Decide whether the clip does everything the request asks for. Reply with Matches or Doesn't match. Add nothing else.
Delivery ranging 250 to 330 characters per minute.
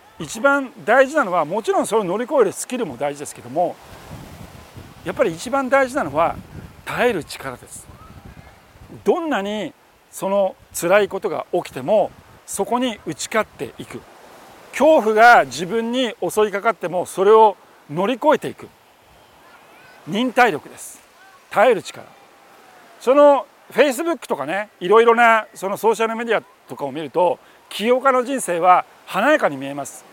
Matches